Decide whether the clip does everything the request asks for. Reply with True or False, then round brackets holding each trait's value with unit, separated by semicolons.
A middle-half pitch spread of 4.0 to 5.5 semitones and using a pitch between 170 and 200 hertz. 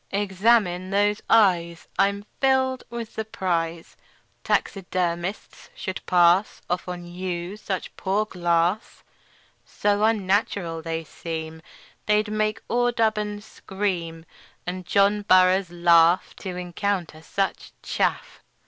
False (3.2 semitones; 190 Hz)